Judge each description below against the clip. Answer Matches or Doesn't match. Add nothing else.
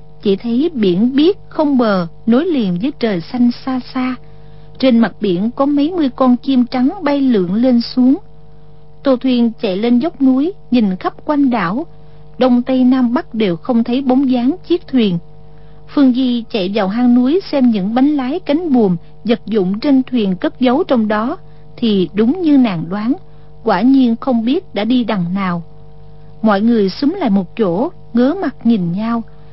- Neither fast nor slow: Matches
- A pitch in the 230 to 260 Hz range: Matches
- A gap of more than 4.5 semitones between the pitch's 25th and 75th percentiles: Matches